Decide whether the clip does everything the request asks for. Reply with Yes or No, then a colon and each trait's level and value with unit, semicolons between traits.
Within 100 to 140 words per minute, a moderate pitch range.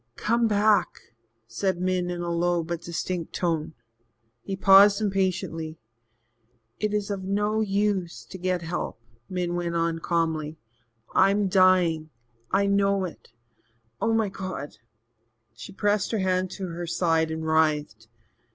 Yes: slow, 135 wpm; average, 3.1 semitones